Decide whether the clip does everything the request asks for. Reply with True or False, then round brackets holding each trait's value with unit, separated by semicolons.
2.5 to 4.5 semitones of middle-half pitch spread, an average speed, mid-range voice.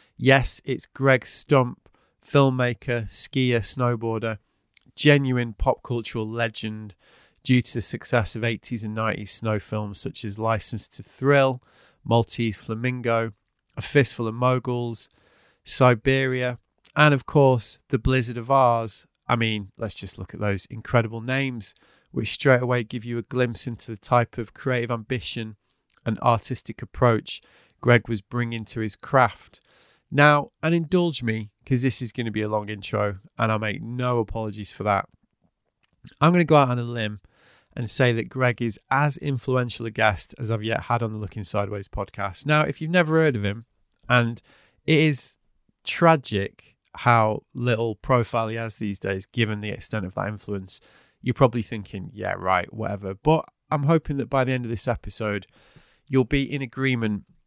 False (3.1 semitones; 170 wpm; 120 Hz)